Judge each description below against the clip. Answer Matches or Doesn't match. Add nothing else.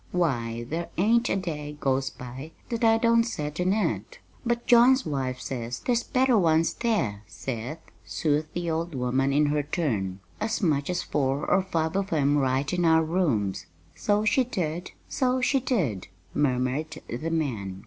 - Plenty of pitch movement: Matches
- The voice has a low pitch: Doesn't match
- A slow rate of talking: Doesn't match